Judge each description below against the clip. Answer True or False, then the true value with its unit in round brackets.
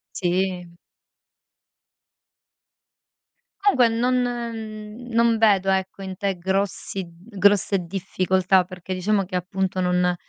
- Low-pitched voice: False (195 Hz)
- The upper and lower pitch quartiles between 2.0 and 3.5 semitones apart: True (2.9 semitones)